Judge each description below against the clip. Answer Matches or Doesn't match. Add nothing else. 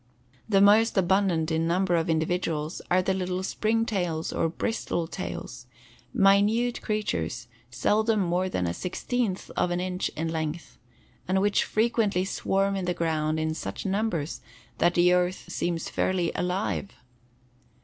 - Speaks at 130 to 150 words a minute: Matches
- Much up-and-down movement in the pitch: Doesn't match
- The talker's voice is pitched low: Doesn't match